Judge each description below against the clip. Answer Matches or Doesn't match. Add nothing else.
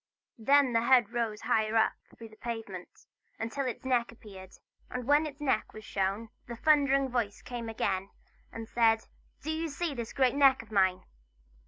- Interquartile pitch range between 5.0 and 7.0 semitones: Doesn't match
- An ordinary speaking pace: Matches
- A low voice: Doesn't match